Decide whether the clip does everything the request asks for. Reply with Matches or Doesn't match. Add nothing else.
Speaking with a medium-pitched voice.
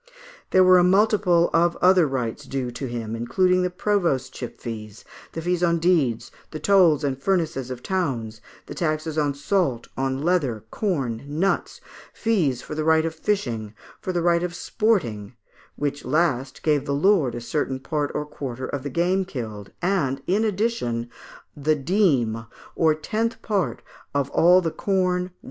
Matches